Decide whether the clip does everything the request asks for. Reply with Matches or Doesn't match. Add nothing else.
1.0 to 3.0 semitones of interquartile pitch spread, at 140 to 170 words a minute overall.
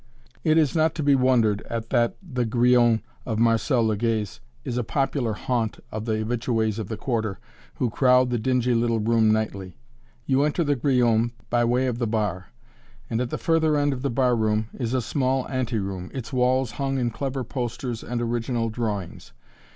Doesn't match